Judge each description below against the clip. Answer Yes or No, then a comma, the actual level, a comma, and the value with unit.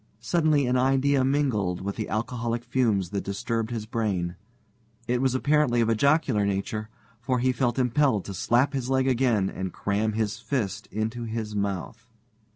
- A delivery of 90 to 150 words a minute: No, average, 165 wpm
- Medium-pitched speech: No, low, 115 Hz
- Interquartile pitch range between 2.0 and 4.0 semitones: Yes, average, 3.7 semitones